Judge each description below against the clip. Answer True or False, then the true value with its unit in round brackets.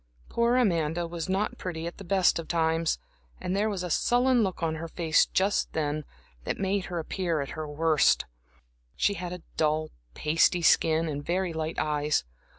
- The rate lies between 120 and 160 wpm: False (180 wpm)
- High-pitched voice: False (165 Hz)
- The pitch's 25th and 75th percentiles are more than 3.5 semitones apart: False (3.1 semitones)